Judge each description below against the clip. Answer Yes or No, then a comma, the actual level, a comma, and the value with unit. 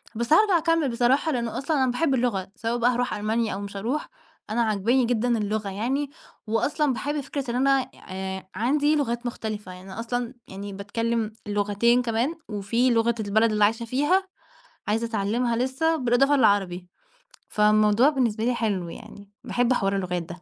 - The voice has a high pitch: Yes, high, 235 Hz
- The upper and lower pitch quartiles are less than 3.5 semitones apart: No, average, 3.9 semitones